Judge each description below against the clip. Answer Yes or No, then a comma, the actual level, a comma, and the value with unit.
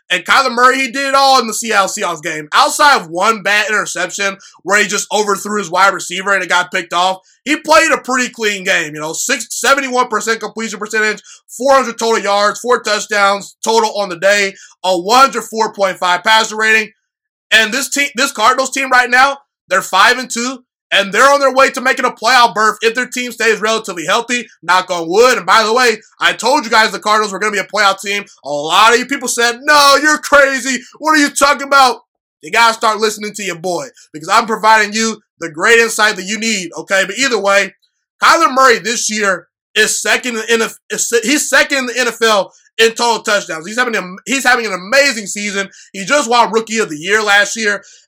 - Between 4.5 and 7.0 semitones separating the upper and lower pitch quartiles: No, average, 4.0 semitones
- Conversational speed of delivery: No, fast, 215 wpm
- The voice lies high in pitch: Yes, high, 220 Hz